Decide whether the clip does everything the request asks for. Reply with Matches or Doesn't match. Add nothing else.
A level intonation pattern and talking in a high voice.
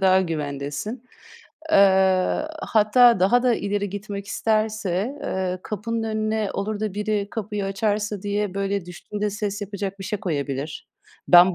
Matches